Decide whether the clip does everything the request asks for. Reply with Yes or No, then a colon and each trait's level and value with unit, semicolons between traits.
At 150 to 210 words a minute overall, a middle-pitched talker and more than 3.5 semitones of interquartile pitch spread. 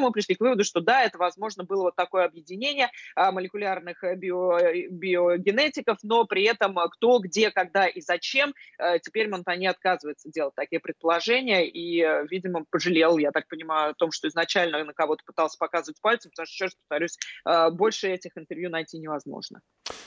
No: fast, 160 wpm; medium, 180 Hz; average, 3.2 semitones